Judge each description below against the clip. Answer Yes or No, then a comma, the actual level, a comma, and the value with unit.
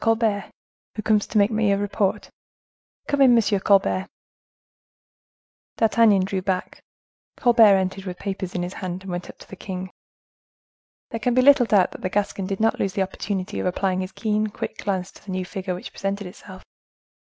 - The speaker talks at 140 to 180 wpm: No, average, 190 wpm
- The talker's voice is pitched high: Yes, high, 195 Hz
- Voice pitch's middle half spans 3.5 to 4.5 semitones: No, narrow, 2.5 semitones